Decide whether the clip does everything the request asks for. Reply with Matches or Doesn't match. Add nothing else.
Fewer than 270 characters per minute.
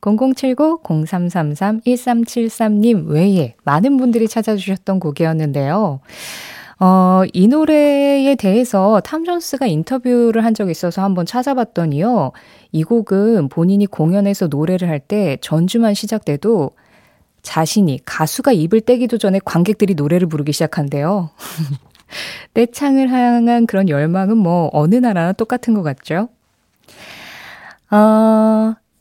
Matches